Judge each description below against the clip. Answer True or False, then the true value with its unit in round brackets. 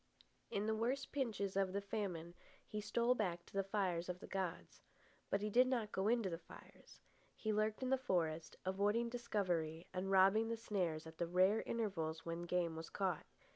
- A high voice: True (195 Hz)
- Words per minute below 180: False (190 wpm)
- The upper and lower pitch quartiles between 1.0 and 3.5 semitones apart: False (3.9 semitones)